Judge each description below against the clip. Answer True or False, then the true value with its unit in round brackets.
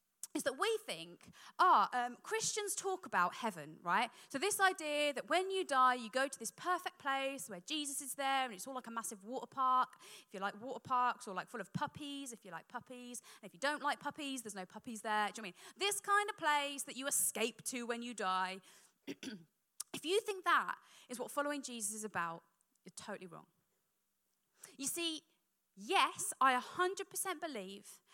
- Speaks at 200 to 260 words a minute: True (205 wpm)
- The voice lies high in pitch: True (260 Hz)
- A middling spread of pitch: False (5.7 semitones)